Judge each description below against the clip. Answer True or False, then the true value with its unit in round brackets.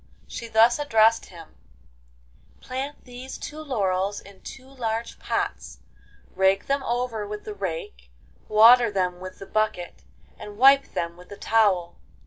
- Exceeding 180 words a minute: False (140 wpm)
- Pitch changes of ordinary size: True (4.5 semitones)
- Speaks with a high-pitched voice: True (215 Hz)